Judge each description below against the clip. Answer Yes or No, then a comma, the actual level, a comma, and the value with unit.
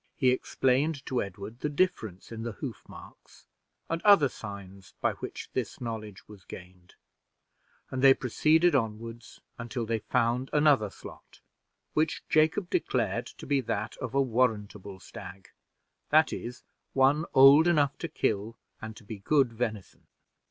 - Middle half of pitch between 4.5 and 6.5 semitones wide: Yes, average, 4.9 semitones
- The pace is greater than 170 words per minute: No, average, 145 wpm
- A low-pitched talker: Yes, low, 120 Hz